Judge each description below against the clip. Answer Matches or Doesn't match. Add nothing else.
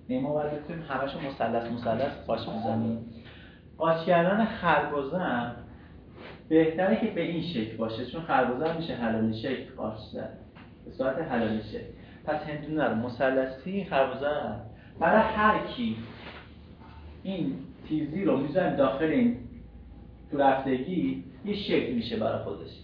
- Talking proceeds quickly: Doesn't match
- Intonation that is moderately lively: Doesn't match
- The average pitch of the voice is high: Doesn't match